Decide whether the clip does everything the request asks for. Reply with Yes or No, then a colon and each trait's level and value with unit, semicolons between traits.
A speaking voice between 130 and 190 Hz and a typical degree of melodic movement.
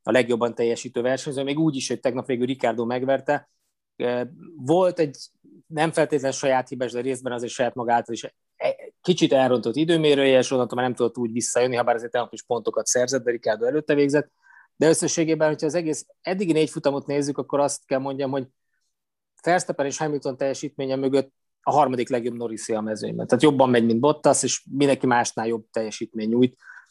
Yes: low, 135 Hz; average, 3.5 semitones